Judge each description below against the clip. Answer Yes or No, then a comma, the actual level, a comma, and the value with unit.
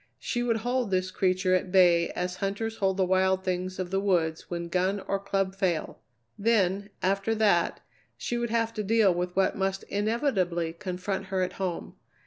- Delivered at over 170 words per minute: Yes, average, 180 wpm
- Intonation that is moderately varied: No, narrow, 2.0 semitones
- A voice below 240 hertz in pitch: Yes, high, 190 Hz